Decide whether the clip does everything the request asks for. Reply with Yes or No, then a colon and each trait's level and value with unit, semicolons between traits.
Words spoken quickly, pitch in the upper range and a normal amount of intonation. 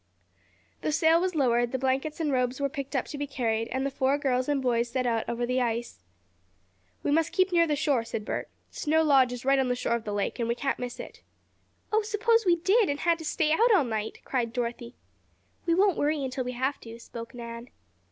Yes: fast, 230 wpm; very high, 265 Hz; average, 4.4 semitones